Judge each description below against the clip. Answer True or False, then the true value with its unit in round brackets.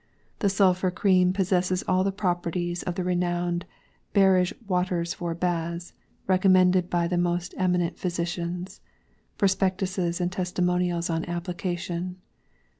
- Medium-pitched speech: True (180 Hz)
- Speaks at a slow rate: True (115 wpm)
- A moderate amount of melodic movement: False (1.1 semitones)